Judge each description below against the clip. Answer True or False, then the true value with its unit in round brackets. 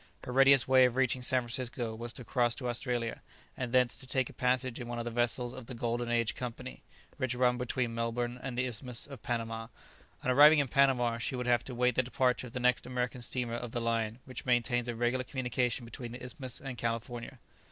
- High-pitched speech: False (125 Hz)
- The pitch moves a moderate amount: False (1.4 semitones)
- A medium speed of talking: False (225 wpm)